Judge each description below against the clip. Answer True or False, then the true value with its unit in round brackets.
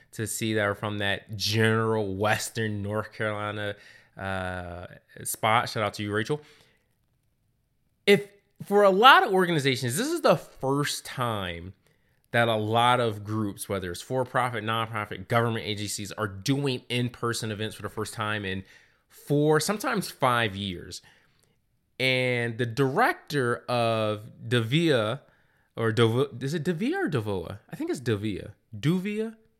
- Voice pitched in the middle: False (115 Hz)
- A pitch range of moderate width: True (4.3 semitones)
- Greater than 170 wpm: False (140 wpm)